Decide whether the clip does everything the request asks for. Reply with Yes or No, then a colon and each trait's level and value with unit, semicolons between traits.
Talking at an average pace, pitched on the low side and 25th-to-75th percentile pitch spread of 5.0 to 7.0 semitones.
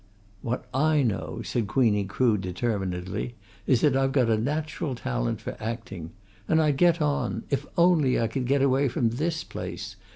Yes: average, 170 wpm; low, 125 Hz; average, 5.3 semitones